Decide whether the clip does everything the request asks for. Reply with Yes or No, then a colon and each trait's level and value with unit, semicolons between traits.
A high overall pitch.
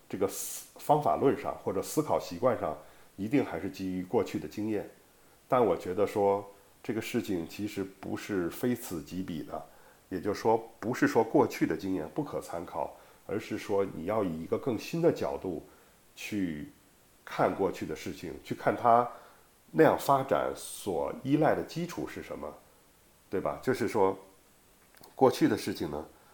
No: low, 100 Hz